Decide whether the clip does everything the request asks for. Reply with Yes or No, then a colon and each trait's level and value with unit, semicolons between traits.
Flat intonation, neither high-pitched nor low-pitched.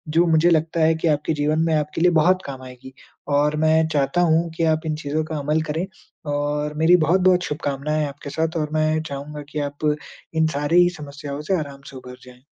Yes: narrow, 1.9 semitones; medium, 155 Hz